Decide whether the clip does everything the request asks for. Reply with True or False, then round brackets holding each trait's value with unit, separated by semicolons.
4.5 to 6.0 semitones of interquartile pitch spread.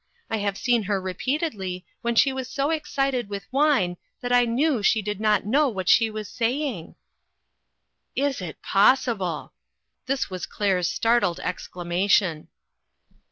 True (5.6 semitones)